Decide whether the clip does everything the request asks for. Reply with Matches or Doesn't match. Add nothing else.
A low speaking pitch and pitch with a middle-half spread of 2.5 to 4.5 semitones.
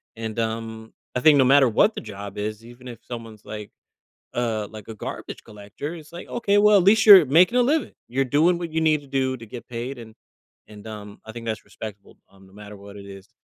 Doesn't match